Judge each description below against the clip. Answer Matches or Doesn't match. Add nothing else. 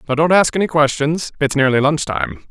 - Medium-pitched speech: Matches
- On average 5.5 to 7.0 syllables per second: Matches